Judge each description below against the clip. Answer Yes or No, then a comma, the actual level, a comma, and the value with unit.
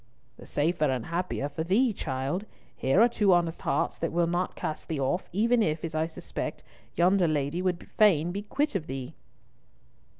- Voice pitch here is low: No, medium, 170 Hz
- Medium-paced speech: Yes, average, 190 wpm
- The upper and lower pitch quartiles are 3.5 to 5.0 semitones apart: Yes, average, 3.9 semitones